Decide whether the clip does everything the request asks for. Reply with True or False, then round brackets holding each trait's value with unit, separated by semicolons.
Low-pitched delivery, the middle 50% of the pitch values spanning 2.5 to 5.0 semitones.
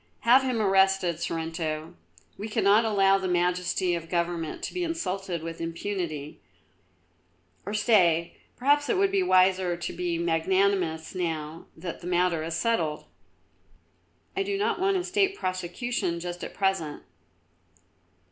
False (180 Hz; 4.0 semitones)